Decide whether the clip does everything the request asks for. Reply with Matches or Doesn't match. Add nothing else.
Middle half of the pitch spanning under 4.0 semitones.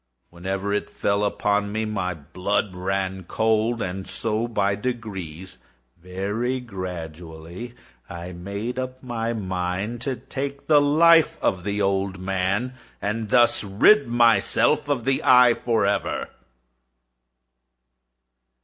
Doesn't match